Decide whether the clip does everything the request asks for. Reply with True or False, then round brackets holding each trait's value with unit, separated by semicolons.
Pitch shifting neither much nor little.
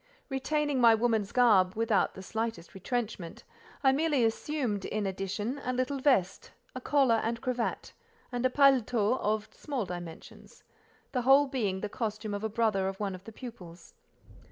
True (4.2 semitones)